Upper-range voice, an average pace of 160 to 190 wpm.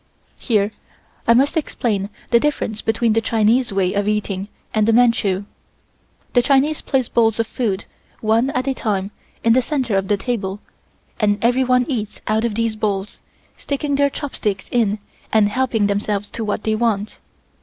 Yes: high, 225 Hz; average, 170 wpm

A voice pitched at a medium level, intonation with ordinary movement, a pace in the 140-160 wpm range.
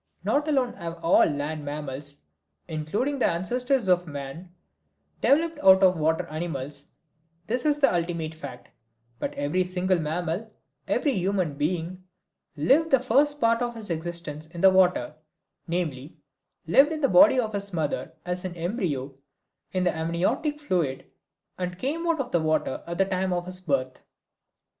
No: medium, 180 Hz; wide, 6.6 semitones; average, 155 wpm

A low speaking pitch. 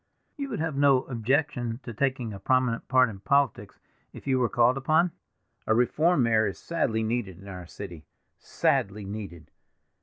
Yes: low, 120 Hz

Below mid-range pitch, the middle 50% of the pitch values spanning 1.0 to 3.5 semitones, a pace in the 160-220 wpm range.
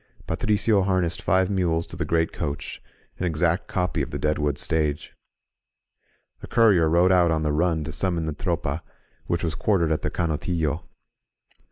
Yes: very low, 85 Hz; narrow, 2.6 semitones; average, 170 wpm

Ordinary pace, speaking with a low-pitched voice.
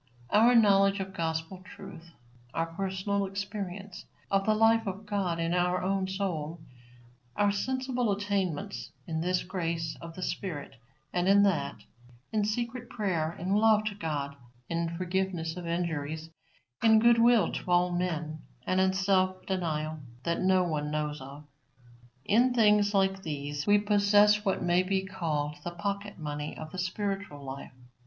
No: average, 150 wpm; medium, 185 Hz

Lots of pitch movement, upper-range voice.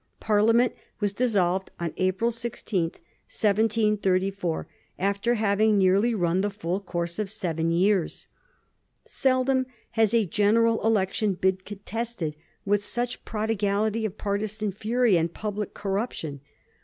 No: average, 2.9 semitones; high, 205 Hz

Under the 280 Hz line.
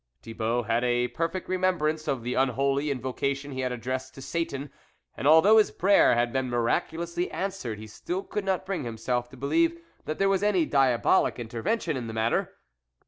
Yes: medium, 140 Hz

